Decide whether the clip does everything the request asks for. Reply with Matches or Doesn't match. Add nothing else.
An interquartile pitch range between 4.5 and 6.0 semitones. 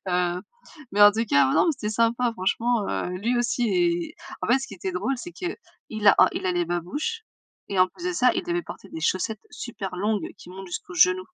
Matches